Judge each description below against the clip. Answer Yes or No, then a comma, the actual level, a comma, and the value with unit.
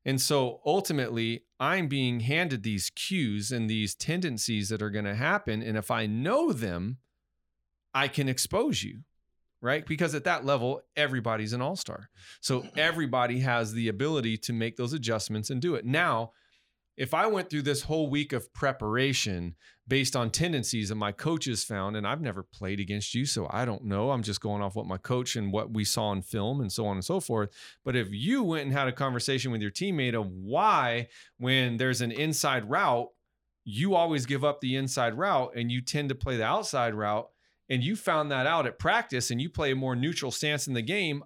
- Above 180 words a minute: Yes, fast, 205 wpm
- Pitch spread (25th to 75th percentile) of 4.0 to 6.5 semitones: Yes, average, 4.5 semitones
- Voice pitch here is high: No, low, 125 Hz